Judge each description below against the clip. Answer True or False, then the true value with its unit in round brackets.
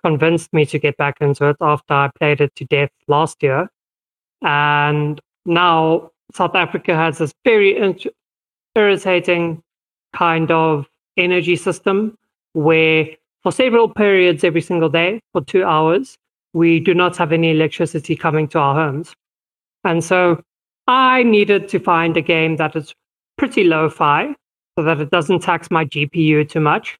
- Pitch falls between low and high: True (165 Hz)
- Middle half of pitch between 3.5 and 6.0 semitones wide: False (2.6 semitones)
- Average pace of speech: True (155 wpm)